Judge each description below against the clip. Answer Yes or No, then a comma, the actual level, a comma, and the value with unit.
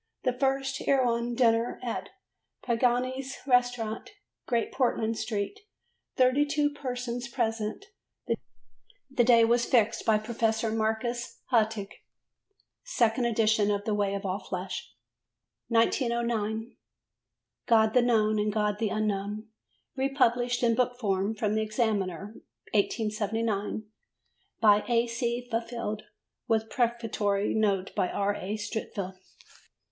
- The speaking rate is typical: No, slow, 110 wpm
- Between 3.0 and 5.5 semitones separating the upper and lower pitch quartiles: No, narrow, 2.4 semitones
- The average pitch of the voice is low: No, high, 225 Hz